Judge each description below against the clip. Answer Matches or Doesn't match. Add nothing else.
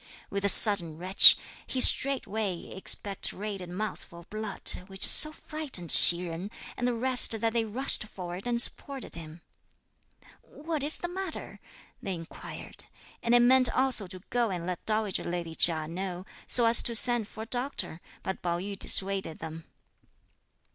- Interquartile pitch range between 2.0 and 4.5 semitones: Doesn't match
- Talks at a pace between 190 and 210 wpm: Doesn't match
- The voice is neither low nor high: Doesn't match